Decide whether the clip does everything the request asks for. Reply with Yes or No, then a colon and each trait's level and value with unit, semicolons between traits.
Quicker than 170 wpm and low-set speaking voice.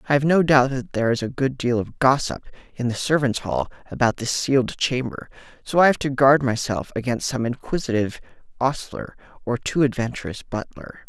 Yes: average, 180 wpm; low, 125 Hz